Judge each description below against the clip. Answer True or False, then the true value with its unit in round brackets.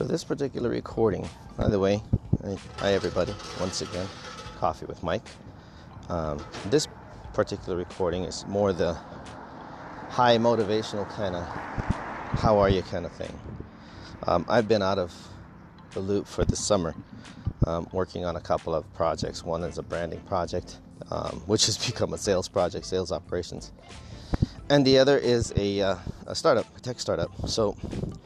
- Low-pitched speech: True (100 Hz)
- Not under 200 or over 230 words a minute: False (155 wpm)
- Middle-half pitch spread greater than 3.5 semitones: True (4.3 semitones)